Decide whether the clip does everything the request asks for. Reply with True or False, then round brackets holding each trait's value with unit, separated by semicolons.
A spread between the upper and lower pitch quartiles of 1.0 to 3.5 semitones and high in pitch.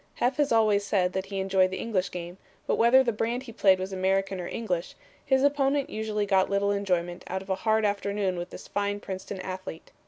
True (2.8 semitones; 200 Hz)